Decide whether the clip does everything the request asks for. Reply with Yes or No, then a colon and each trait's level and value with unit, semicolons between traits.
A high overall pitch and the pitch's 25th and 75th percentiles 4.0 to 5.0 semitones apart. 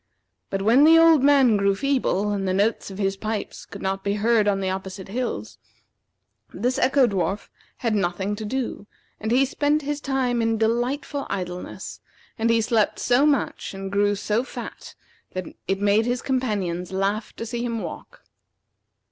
Yes: high, 215 Hz; average, 4.4 semitones